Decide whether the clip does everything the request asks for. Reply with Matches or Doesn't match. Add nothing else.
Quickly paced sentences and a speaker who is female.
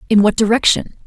Doesn't match